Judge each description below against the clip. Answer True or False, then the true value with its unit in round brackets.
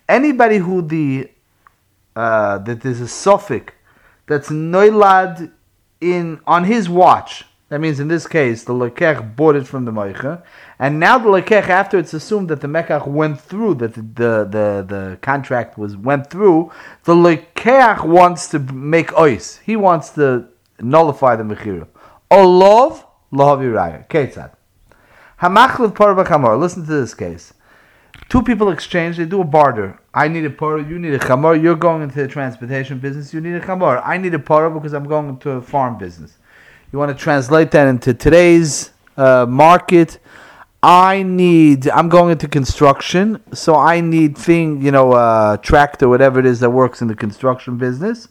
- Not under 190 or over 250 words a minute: False (170 wpm)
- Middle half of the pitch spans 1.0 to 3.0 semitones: False (5.2 semitones)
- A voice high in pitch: False (150 Hz)